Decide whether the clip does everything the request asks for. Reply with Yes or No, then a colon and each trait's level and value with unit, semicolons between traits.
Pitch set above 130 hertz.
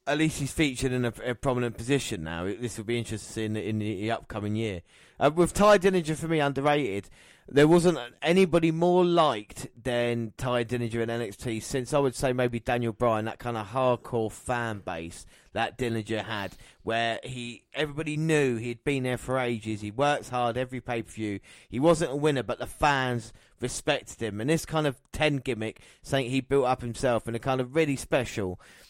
No: low, 125 Hz